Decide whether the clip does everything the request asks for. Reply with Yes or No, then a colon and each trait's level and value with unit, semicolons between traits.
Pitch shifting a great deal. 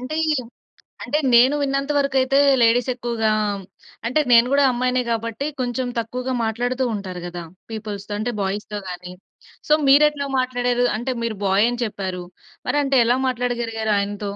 No: average, 3.2 semitones